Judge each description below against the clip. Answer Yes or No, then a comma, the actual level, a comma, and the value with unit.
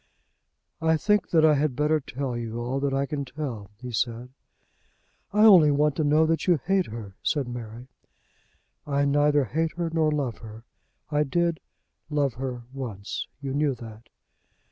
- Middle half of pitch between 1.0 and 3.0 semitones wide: No, average, 4.2 semitones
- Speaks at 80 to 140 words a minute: No, average, 165 wpm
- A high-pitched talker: No, medium, 140 Hz